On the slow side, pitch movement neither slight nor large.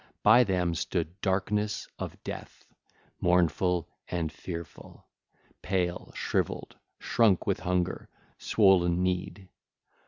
No: slow, 95 wpm; narrow, 1.8 semitones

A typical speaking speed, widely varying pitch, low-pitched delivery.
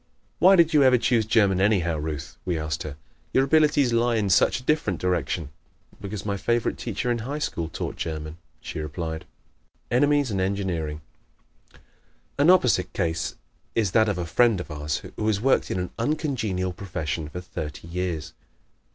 Yes: average, 170 wpm; wide, 6.7 semitones; very low, 95 Hz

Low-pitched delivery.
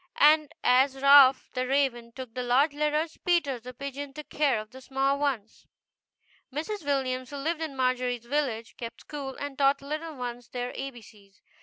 No: very high, 270 Hz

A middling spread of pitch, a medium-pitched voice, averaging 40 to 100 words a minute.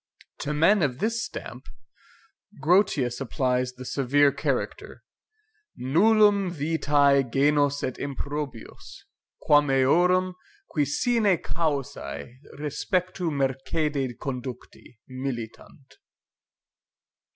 Yes: average, 4.4 semitones; medium, 145 Hz; slow, 85 wpm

